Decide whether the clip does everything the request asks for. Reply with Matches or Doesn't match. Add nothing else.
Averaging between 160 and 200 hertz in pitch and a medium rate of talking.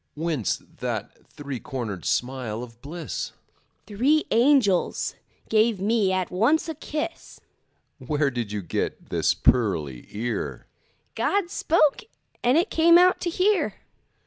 Doesn't match